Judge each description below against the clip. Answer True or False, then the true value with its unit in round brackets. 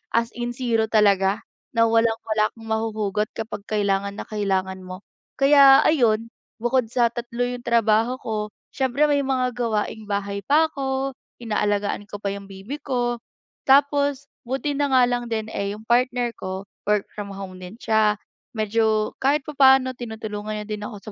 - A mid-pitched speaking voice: False (225 Hz)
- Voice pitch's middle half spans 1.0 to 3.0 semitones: False (3.5 semitones)